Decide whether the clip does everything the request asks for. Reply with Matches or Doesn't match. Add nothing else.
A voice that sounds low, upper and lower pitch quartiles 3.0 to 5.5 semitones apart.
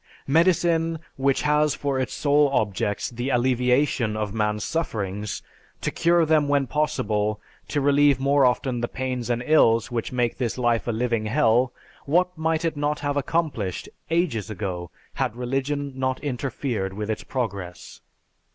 Matches